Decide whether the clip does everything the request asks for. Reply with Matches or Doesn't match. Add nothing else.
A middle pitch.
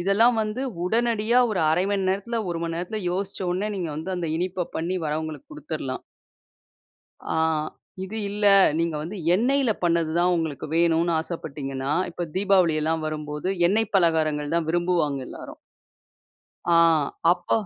Matches